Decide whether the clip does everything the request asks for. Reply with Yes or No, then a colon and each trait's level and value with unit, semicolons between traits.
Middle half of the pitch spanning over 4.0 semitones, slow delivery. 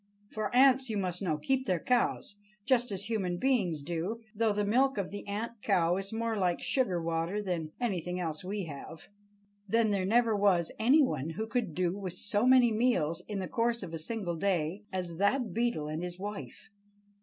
No: average, 4.7 semitones; average, 195 wpm